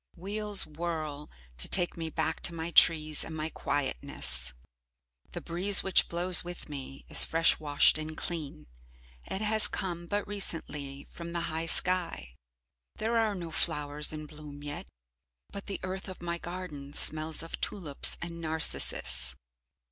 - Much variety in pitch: No, average, 3.1 semitones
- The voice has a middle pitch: Yes, medium, 165 Hz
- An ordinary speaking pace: Yes, average, 150 wpm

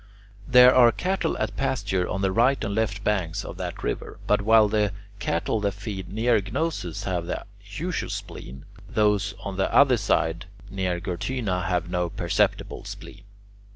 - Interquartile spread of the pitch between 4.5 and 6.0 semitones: No, average, 3.5 semitones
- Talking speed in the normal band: Yes, average, 160 wpm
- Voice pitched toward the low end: Yes, low, 100 Hz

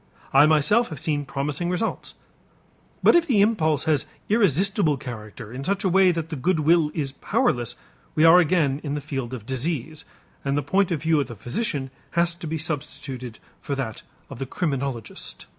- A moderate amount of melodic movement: Yes, average, 4.3 semitones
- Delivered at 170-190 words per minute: Yes, average, 185 wpm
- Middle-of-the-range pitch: Yes, medium, 150 Hz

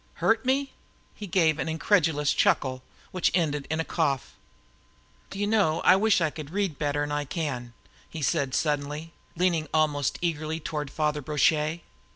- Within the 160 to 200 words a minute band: Yes, average, 165 wpm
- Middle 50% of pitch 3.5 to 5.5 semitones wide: No, average, 2.8 semitones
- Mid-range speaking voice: Yes, medium, 155 Hz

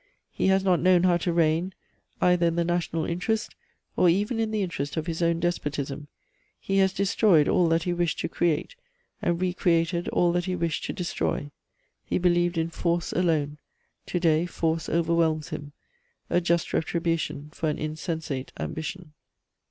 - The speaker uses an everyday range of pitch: No, narrow, 1.9 semitones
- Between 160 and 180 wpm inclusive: Yes, average, 170 wpm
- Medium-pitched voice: Yes, medium, 170 Hz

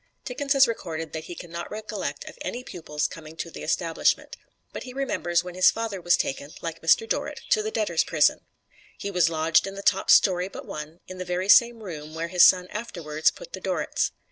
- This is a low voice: No, medium, 180 Hz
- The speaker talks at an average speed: No, fast, 215 wpm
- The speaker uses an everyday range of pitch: Yes, average, 4.7 semitones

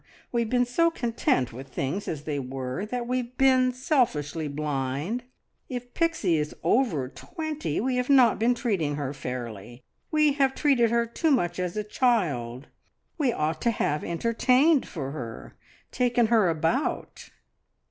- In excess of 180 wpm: No, average, 155 wpm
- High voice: Yes, high, 220 Hz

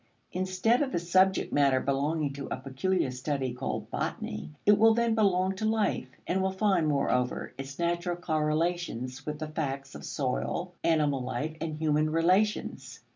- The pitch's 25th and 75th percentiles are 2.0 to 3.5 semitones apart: No, average, 5.2 semitones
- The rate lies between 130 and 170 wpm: Yes, average, 160 wpm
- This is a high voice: No, medium, 160 Hz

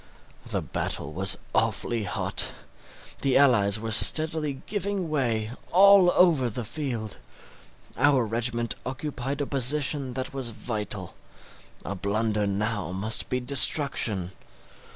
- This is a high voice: No, low, 125 Hz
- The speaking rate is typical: No, slow, 115 wpm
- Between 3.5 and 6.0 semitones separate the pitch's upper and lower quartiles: Yes, average, 4.9 semitones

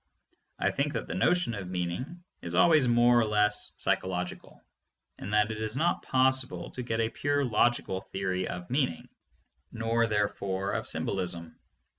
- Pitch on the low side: Yes, low, 110 Hz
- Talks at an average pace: Yes, average, 155 wpm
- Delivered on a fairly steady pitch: No, average, 5.2 semitones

